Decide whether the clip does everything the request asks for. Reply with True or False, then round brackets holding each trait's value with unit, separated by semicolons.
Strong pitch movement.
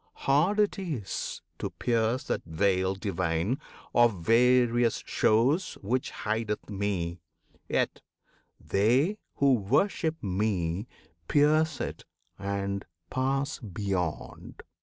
True (5.7 semitones)